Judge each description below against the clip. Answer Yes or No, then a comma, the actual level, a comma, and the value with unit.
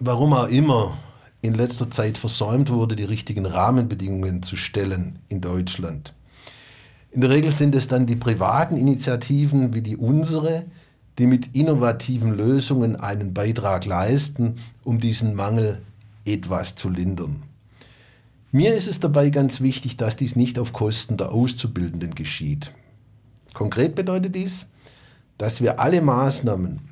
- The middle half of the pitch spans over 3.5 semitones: Yes, average, 4.2 semitones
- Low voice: Yes, low, 120 Hz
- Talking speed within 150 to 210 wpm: No, average, 135 wpm